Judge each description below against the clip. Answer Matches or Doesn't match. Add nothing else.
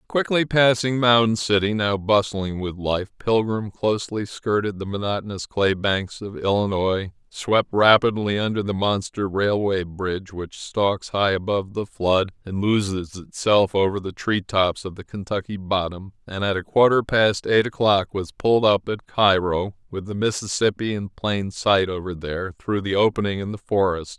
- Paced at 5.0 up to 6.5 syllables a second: Doesn't match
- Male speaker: Matches